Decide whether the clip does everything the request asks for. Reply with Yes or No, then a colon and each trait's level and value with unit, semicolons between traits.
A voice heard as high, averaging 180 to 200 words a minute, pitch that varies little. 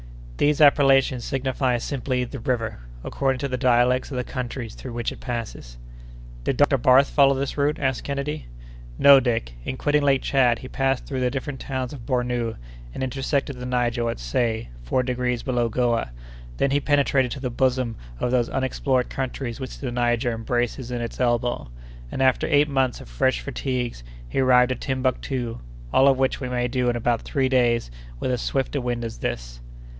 No: low, 125 Hz; average, 190 wpm; narrow, 2.1 semitones